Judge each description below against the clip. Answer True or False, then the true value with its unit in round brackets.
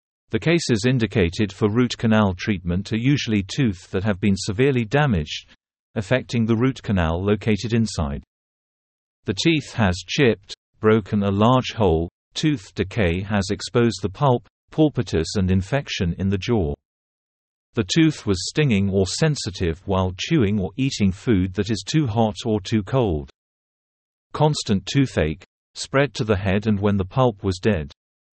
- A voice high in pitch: False (110 Hz)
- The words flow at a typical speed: False (150 wpm)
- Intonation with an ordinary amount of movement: True (4.5 semitones)